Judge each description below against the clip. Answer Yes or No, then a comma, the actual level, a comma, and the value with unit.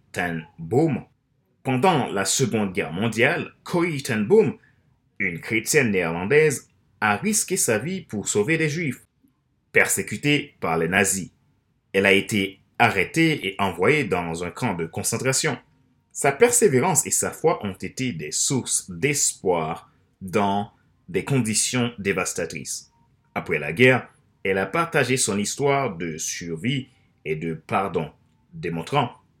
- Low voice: Yes, low, 125 Hz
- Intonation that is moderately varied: No, wide, 7.7 semitones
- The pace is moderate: No, slow, 130 wpm